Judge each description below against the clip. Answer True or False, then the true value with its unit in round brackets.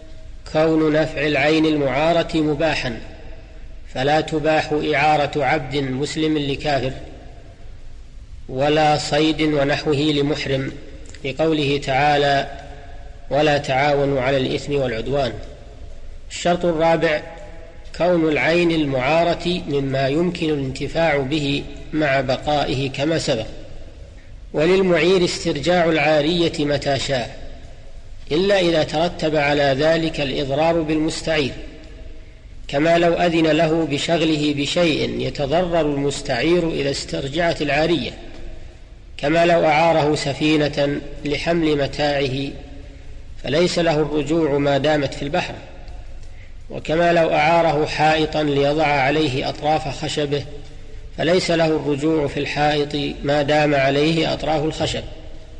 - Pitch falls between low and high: True (150 Hz)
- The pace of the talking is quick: False (95 wpm)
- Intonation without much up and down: True (2.3 semitones)